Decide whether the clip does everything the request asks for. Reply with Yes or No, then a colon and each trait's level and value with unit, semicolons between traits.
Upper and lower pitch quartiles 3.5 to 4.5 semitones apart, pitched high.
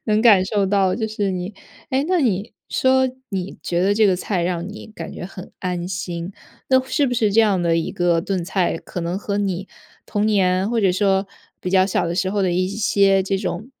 No: average, 2.7 semitones; high, 195 Hz